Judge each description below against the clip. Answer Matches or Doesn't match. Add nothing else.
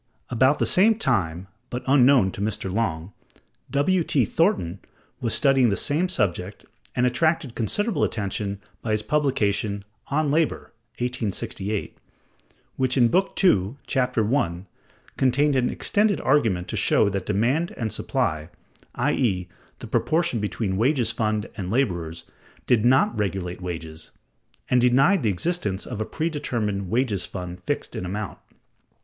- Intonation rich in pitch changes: Matches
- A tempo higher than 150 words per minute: Doesn't match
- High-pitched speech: Doesn't match